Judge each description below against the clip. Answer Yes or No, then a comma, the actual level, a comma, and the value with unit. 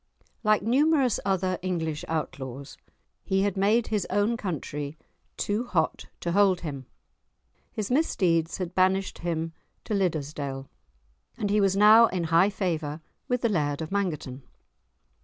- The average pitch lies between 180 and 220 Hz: Yes, medium, 185 Hz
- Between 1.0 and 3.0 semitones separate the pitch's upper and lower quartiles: No, average, 4.5 semitones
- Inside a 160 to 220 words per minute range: No, average, 140 wpm